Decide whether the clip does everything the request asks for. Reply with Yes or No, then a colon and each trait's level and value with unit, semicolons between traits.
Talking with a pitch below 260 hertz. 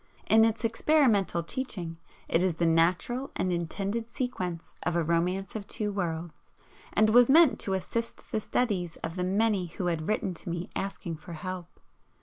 Yes: medium, 185 Hz